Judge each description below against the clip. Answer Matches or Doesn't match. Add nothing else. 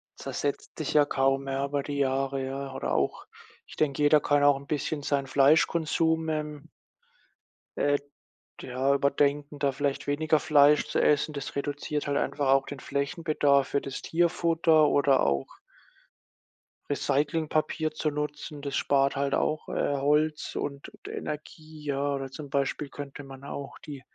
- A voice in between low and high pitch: Matches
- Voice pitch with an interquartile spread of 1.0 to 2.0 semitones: Matches